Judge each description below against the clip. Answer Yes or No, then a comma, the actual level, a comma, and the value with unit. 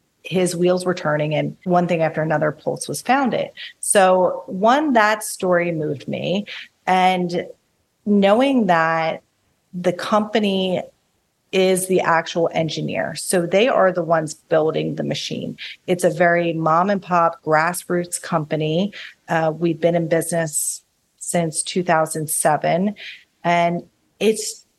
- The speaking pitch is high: No, medium, 175 Hz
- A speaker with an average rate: No, slow, 125 wpm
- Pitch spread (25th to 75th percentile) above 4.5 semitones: No, narrow, 2.5 semitones